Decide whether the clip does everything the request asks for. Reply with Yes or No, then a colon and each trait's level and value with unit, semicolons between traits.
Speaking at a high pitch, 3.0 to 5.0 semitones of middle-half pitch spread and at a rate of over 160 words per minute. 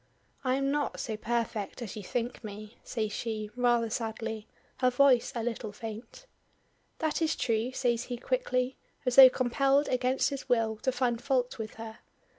No: high, 240 Hz; narrow, 2.6 semitones; average, 170 wpm